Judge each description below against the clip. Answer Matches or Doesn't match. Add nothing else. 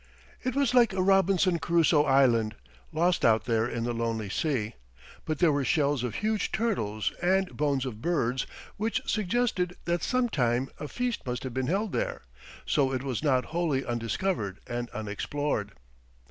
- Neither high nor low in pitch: Matches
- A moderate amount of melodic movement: Doesn't match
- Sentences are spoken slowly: Doesn't match